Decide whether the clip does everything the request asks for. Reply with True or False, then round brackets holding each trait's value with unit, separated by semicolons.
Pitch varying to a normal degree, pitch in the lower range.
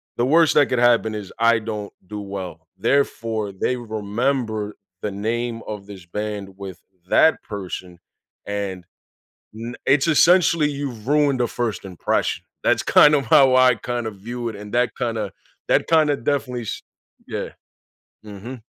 True (4.0 semitones; 115 Hz)